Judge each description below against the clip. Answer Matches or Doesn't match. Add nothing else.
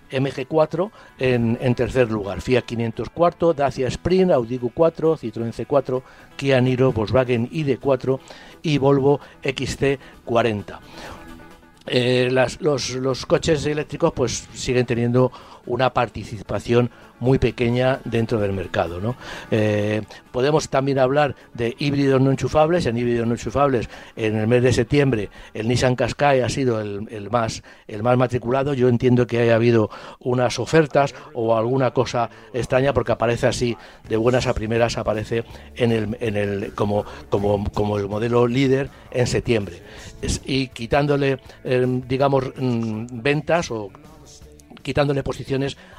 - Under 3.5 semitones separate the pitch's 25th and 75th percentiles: Matches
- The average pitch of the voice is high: Doesn't match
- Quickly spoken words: Doesn't match